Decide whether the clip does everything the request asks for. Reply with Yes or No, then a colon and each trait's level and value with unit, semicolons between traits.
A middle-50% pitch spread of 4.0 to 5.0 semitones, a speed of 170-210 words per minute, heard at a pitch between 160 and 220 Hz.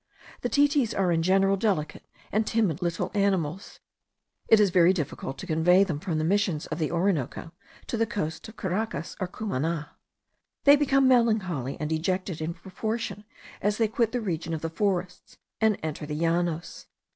Yes: average, 4.7 semitones; average, 175 wpm; medium, 185 Hz